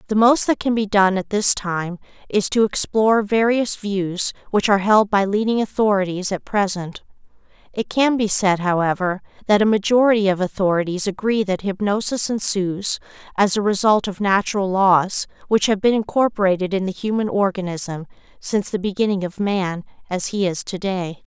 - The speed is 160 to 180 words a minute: Yes, average, 165 wpm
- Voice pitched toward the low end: No, high, 200 Hz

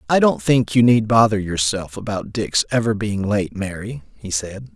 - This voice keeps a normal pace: Yes, average, 190 wpm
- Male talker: Yes, male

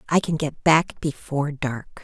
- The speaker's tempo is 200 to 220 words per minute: No, average, 175 wpm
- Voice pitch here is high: No, medium, 150 Hz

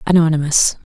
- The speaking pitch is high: No, medium, 170 Hz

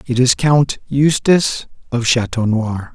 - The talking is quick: No, average, 140 wpm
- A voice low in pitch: Yes, low, 125 Hz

